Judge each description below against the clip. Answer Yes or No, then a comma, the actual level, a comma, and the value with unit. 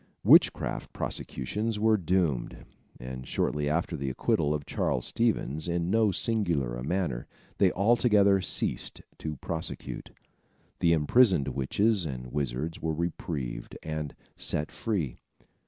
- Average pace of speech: No, slow, 120 wpm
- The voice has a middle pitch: No, very low, 80 Hz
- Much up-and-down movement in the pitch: Yes, wide, 6.1 semitones